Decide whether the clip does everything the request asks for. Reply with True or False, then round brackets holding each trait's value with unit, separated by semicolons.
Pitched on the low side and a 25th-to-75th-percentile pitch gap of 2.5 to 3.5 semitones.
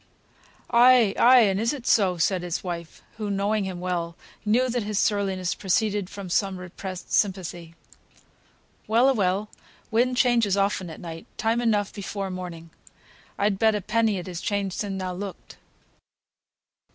False (200 Hz; 3.2 semitones)